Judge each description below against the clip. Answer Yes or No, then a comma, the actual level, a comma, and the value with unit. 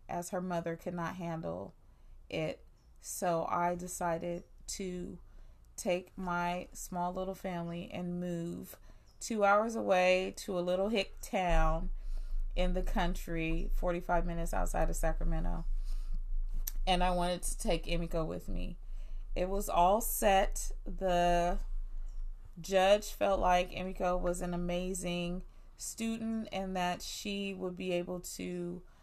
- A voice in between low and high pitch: Yes, medium, 180 Hz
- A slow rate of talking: Yes, slow, 130 wpm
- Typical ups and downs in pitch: No, narrow, 1.4 semitones